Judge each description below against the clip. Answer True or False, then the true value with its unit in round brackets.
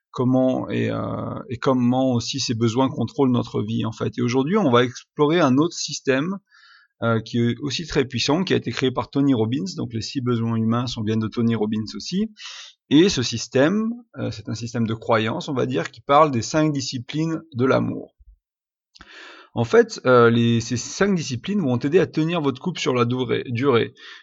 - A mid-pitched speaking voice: False (125 Hz)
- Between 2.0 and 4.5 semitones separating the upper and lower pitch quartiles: True (4.2 semitones)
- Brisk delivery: False (200 wpm)